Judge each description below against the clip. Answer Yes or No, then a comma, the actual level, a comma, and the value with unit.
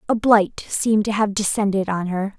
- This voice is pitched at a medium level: No, high, 205 Hz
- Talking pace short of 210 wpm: Yes, average, 200 wpm